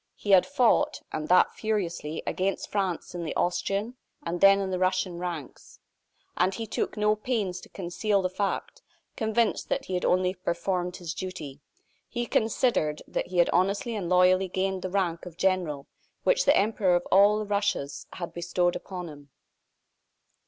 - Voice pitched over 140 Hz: Yes, medium, 185 Hz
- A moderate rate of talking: Yes, average, 170 wpm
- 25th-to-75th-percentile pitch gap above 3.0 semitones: No, narrow, 2.6 semitones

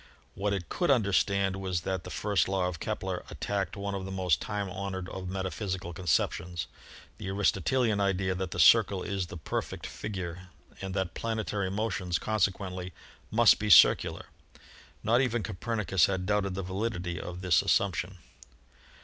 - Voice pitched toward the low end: Yes, very low, 95 Hz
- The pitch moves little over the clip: Yes, narrow, 2.0 semitones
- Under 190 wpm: Yes, average, 160 wpm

